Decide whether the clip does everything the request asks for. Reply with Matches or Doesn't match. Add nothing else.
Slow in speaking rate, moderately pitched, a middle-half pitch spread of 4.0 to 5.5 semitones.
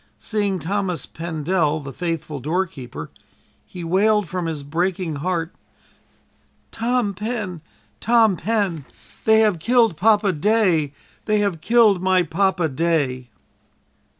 Matches